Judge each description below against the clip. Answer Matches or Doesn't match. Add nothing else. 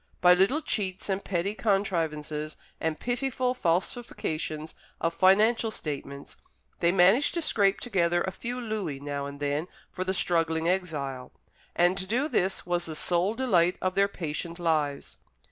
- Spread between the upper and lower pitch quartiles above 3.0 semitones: Matches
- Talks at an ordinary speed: Matches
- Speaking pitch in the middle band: Matches